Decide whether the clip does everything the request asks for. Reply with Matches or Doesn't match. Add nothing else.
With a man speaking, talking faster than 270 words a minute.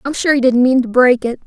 Doesn't match